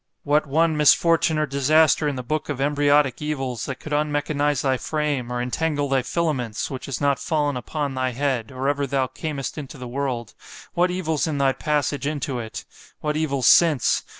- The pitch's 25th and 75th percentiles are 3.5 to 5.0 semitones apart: No, narrow, 2.5 semitones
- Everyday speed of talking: Yes, average, 180 wpm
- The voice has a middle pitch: Yes, medium, 145 Hz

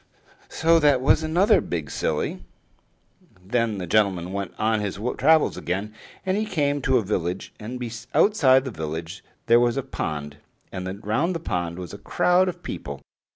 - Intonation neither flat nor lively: No, wide, 8.2 semitones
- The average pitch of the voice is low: Yes, low, 110 Hz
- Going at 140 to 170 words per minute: Yes, average, 165 wpm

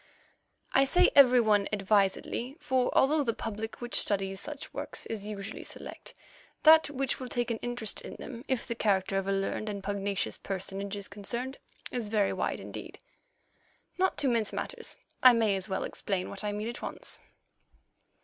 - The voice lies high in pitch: Yes, high, 220 Hz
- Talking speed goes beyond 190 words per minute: No, average, 175 wpm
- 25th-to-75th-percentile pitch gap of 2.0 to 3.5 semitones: No, average, 4.1 semitones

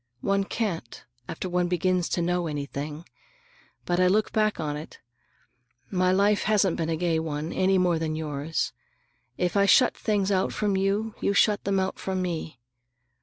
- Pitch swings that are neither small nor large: Yes, average, 3.4 semitones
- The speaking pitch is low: No, medium, 180 Hz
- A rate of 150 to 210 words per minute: Yes, average, 170 wpm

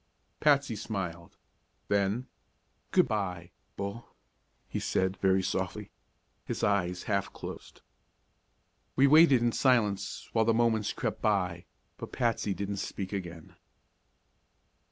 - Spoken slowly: Yes, slow, 115 wpm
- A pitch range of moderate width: Yes, average, 3.8 semitones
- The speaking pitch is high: No, low, 100 Hz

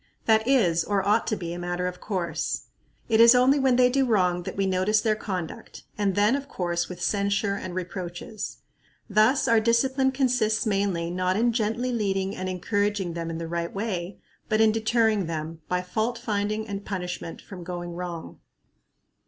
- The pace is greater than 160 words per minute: Yes, average, 180 wpm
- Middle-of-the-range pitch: No, high, 200 Hz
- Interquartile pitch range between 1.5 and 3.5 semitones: No, average, 3.9 semitones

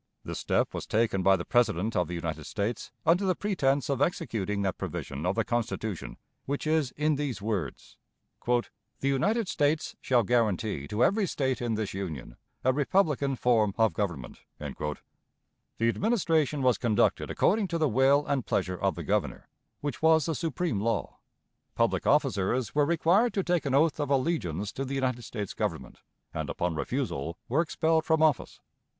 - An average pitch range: No, wide, 7.1 semitones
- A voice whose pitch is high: No, low, 130 Hz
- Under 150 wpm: No, average, 170 wpm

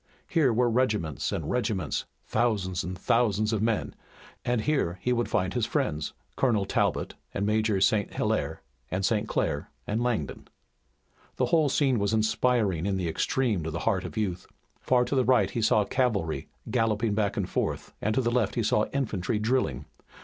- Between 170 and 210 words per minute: Yes, average, 180 wpm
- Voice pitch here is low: Yes, low, 110 Hz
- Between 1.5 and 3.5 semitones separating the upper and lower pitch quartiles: No, average, 4.2 semitones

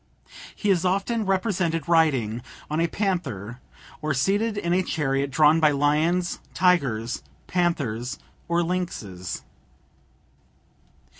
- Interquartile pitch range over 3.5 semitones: Yes, average, 5.1 semitones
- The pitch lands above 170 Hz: No, medium, 165 Hz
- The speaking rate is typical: No, slow, 105 wpm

